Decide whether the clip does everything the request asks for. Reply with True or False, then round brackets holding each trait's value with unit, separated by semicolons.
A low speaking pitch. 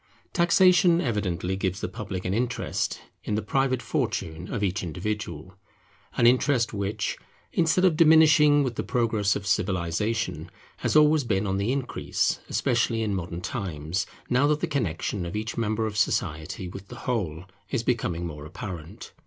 True (105 Hz)